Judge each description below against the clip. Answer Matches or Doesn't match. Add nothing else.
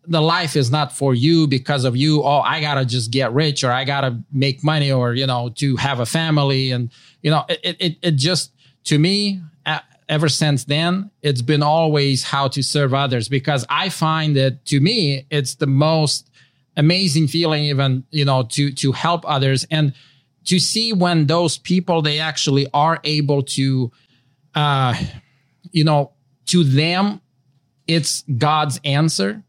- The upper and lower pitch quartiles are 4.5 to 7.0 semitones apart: Doesn't match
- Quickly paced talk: Doesn't match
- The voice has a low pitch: Doesn't match